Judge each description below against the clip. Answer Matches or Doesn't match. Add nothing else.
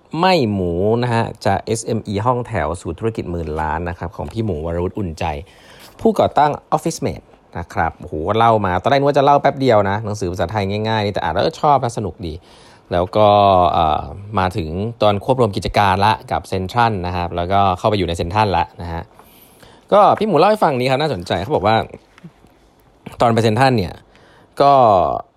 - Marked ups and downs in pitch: Doesn't match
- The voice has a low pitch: Matches